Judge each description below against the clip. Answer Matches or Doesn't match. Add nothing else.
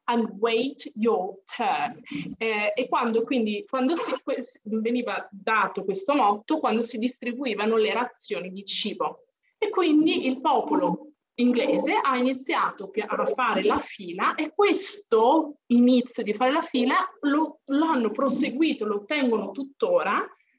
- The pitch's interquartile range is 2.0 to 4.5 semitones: Doesn't match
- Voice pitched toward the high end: Matches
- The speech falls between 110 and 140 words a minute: Matches